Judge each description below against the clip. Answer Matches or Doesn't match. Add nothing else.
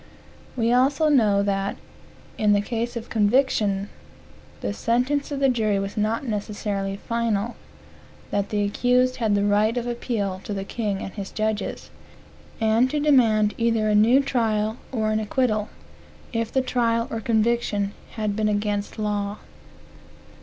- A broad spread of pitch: Doesn't match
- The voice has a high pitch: Matches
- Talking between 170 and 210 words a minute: Doesn't match